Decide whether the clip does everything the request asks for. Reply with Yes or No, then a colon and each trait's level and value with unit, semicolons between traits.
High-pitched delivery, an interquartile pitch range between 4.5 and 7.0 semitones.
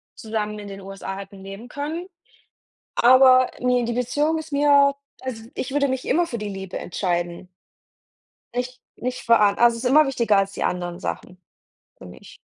Yes: high, 235 Hz; average, 5.0 semitones